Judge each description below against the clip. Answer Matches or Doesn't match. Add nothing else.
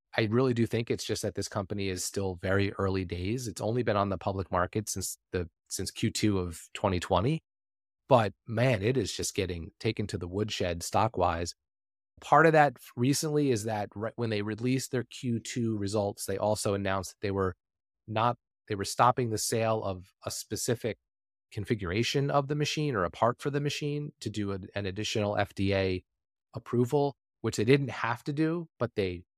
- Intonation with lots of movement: Doesn't match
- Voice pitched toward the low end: Matches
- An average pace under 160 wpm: Doesn't match